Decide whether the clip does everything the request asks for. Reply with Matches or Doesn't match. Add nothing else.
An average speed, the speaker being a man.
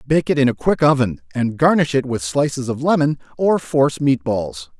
Doesn't match